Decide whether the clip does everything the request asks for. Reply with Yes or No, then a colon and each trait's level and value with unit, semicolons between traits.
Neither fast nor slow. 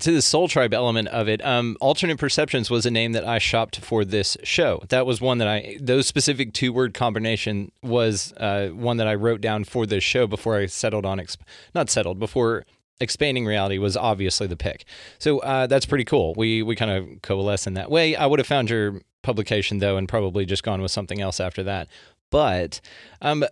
No: fast, 215 wpm